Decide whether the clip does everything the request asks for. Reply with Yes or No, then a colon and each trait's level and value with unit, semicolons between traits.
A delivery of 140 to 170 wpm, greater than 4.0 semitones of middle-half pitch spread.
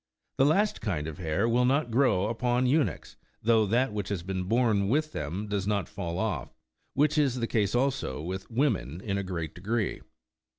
No: average, 185 wpm; average, 5.1 semitones